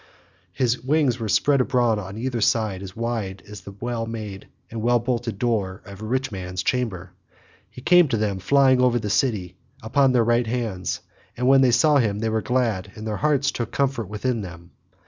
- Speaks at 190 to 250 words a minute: Yes, average, 200 wpm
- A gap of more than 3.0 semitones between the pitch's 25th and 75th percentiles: Yes, average, 3.5 semitones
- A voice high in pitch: No, low, 115 Hz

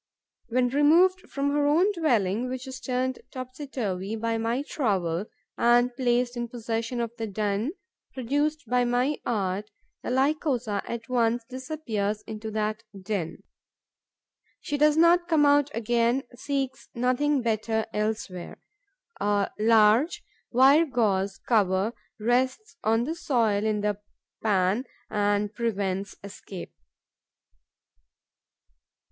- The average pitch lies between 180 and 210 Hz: No, high, 235 Hz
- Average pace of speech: No, slow, 120 wpm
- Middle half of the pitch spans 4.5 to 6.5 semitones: No, average, 4.0 semitones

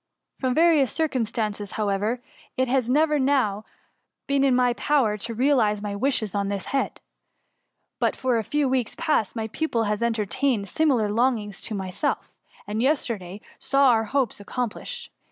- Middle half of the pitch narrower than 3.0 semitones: No, average, 4.6 semitones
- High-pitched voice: Yes, high, 235 Hz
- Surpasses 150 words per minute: Yes, average, 160 wpm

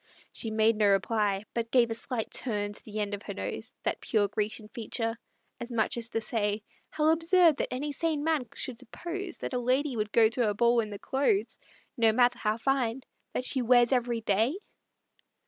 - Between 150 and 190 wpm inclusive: No, average, 200 wpm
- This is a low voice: No, high, 235 Hz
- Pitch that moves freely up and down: No, average, 3.4 semitones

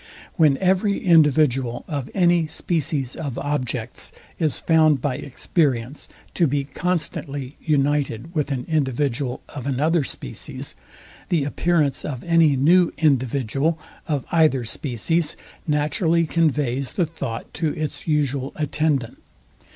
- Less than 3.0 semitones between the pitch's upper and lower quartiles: No, average, 3.3 semitones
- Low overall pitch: No, medium, 150 Hz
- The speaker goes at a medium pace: No, slow, 120 wpm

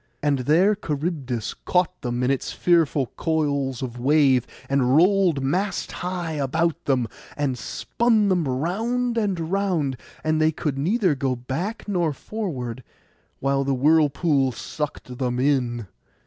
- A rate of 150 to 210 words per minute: No, slow, 135 wpm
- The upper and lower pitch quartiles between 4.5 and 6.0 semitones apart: Yes, average, 5.2 semitones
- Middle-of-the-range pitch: Yes, medium, 150 Hz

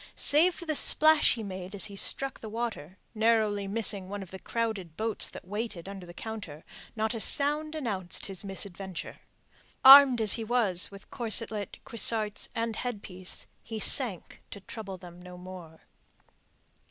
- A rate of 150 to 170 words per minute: Yes, average, 160 wpm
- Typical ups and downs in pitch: Yes, average, 3.5 semitones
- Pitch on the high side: Yes, high, 210 Hz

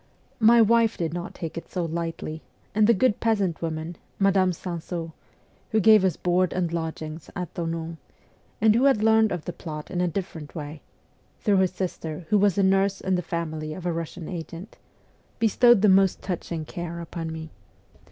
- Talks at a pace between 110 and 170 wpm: No, average, 180 wpm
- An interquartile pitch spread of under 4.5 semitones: Yes, average, 3.3 semitones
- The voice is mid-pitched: Yes, medium, 175 Hz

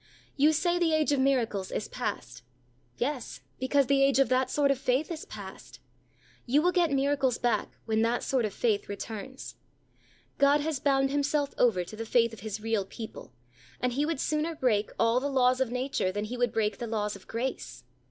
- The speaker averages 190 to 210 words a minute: Yes, average, 200 wpm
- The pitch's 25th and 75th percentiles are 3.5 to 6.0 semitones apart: Yes, average, 4.0 semitones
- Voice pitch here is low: No, very high, 255 Hz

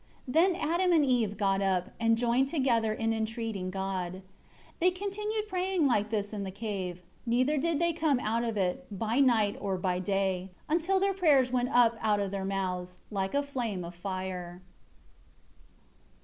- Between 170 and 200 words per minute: Yes, average, 175 wpm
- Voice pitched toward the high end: Yes, high, 225 Hz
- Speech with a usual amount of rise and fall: No, wide, 6.6 semitones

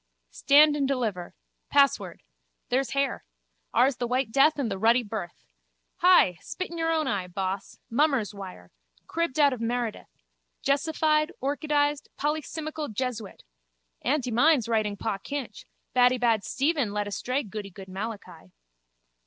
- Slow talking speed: Yes, slow, 130 wpm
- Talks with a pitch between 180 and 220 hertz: No, very high, 250 Hz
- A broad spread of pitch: Yes, wide, 5.7 semitones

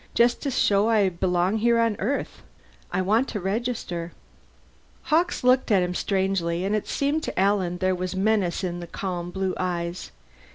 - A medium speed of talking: Yes, average, 170 wpm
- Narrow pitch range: No, average, 3.9 semitones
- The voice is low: No, high, 195 Hz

